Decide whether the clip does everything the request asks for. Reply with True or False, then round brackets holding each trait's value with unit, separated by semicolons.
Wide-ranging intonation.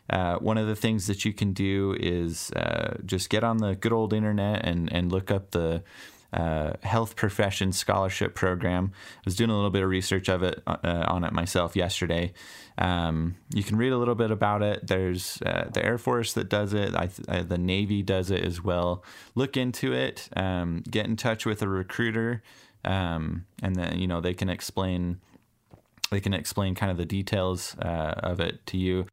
False (3.3 semitones)